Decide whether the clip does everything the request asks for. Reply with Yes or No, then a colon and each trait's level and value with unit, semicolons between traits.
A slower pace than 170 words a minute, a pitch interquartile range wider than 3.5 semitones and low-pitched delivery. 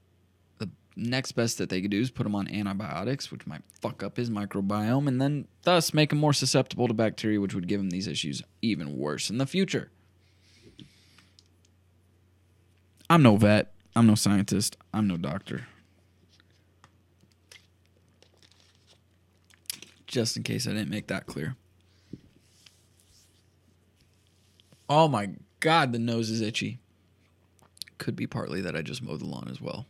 Yes: average, 145 wpm; average, 4.0 semitones; low, 100 Hz